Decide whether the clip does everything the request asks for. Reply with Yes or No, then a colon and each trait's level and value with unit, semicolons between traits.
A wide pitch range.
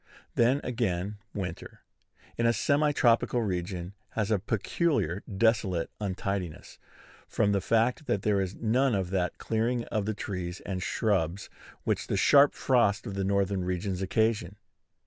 No: average, 3.7 semitones